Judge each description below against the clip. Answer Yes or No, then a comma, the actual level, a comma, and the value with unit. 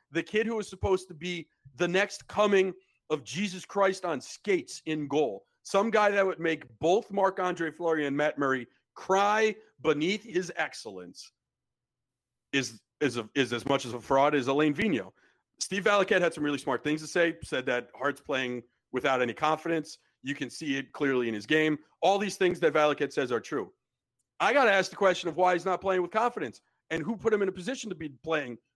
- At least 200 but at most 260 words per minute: Yes, fast, 205 wpm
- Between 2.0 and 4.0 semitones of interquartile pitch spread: No, wide, 5.5 semitones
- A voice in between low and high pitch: Yes, medium, 165 Hz